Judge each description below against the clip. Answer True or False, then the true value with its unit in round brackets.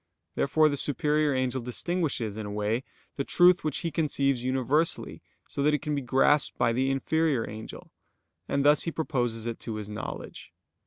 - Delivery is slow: False (175 wpm)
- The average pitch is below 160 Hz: True (135 Hz)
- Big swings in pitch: False (4.2 semitones)